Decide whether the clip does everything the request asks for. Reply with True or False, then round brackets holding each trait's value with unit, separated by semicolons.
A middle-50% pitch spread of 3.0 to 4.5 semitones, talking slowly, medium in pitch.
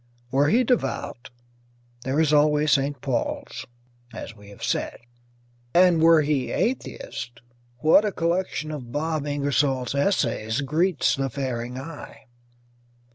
True (3.7 semitones; 125 wpm; 145 Hz)